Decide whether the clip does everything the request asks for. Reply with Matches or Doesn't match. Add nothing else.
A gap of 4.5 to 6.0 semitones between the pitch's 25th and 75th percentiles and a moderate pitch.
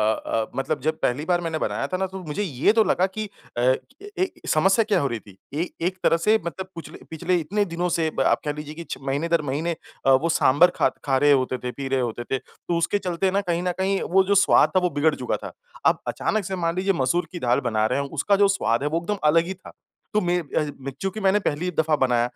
Matches